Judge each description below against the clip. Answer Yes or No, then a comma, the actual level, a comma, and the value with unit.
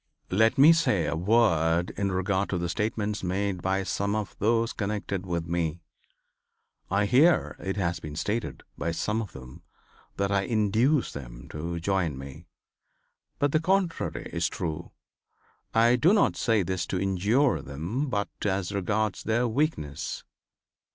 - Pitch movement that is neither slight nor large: Yes, average, 4.6 semitones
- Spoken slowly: No, average, 150 wpm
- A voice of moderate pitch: No, low, 100 Hz